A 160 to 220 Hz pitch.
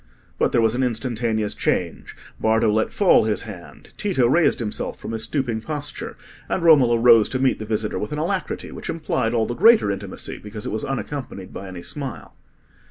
No: low, 115 Hz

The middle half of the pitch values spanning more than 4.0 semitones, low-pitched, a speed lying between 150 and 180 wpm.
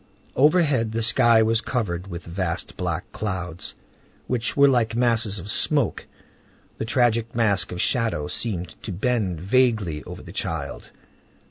No: average, 4.7 semitones; low, 110 Hz; average, 140 wpm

